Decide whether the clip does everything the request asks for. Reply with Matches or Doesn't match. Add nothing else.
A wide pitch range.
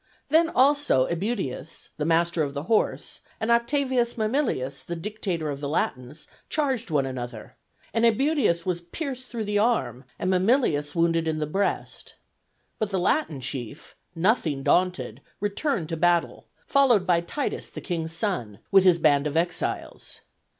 Matches